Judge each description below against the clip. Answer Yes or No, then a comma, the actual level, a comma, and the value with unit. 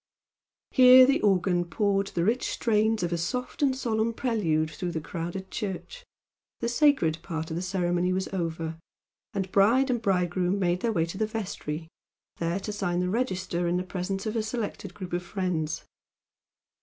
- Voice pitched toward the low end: No, high, 190 Hz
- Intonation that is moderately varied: Yes, average, 4.1 semitones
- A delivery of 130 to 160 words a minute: No, average, 175 wpm